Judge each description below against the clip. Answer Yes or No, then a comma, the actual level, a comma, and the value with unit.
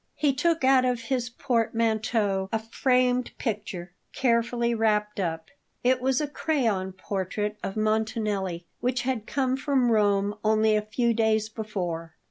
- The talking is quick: No, average, 140 wpm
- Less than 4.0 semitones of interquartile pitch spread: Yes, average, 3.2 semitones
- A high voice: Yes, high, 220 Hz